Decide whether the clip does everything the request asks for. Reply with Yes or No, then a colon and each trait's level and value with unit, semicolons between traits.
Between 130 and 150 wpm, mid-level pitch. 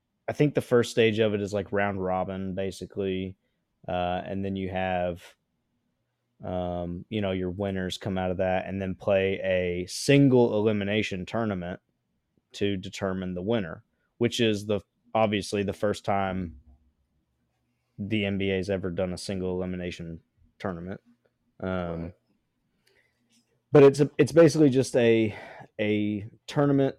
No: average, 140 wpm; low, 100 Hz